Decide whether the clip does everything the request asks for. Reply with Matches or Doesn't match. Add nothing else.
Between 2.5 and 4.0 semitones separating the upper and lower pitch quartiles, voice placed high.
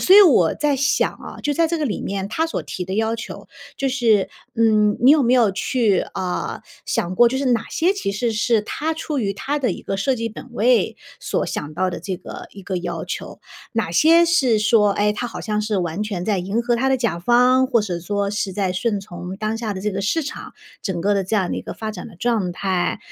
Doesn't match